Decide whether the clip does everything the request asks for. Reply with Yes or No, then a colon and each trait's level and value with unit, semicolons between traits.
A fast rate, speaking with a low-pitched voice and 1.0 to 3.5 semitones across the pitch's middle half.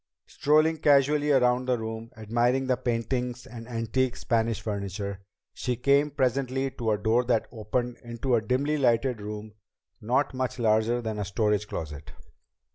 No: average, 155 wpm; low, 120 Hz; average, 2.9 semitones